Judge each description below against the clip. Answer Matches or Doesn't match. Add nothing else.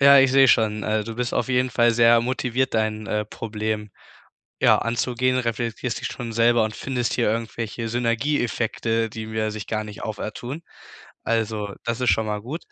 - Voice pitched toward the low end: Matches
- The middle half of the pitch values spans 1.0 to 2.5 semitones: Matches